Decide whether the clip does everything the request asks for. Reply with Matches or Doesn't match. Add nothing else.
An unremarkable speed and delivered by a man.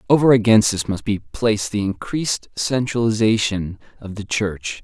Matches